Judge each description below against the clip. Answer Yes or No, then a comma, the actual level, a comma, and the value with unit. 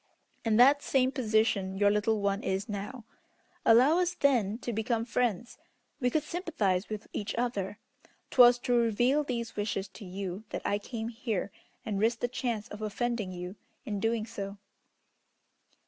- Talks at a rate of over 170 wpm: No, average, 160 wpm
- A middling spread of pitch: Yes, average, 3.2 semitones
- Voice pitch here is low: No, high, 225 Hz